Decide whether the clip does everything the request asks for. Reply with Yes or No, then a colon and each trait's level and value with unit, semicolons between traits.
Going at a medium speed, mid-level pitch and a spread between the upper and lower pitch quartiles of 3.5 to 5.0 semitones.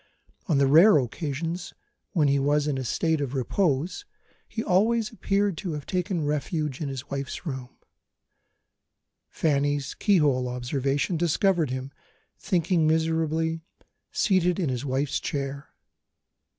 No: slow, 125 wpm; medium, 150 Hz; average, 4.0 semitones